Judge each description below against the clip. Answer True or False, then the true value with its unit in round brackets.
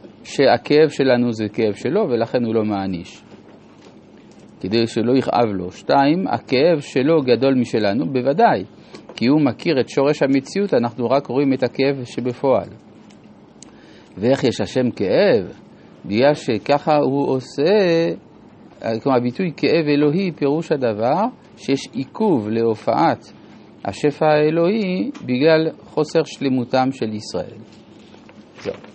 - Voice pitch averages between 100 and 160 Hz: True (135 Hz)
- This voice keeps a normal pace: True (115 wpm)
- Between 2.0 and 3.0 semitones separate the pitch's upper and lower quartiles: False (4.2 semitones)